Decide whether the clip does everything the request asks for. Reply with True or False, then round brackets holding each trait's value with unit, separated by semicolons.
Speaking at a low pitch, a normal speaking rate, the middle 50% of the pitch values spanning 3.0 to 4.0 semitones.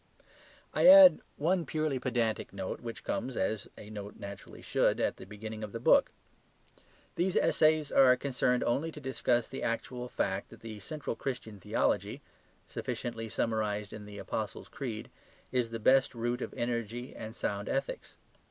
True (120 Hz; 160 wpm; 3.7 semitones)